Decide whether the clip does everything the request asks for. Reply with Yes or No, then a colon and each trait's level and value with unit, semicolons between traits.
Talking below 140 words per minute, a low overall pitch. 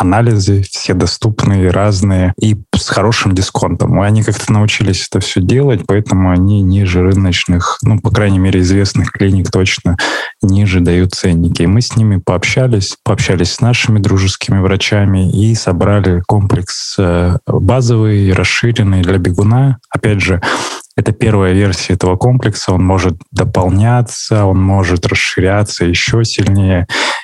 Yes: average, 130 wpm; low, 100 Hz